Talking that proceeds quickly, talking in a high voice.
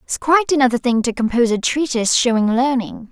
No: average, 190 wpm; very high, 250 Hz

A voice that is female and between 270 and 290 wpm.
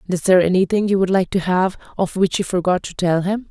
Yes: female; fast, 275 wpm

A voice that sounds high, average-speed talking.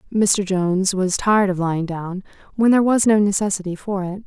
Yes: high, 195 Hz; average, 195 wpm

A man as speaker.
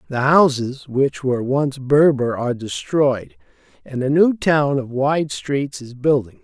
Yes: male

